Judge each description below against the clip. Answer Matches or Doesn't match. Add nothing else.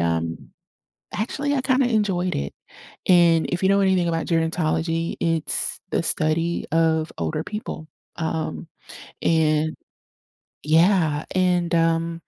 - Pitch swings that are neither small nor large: Doesn't match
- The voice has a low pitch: Doesn't match